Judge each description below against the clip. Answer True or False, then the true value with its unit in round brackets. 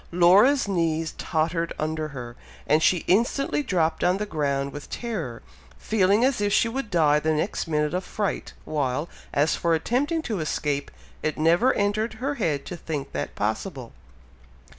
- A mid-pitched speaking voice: True (165 Hz)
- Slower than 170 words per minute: True (160 wpm)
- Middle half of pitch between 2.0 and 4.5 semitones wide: False (5.6 semitones)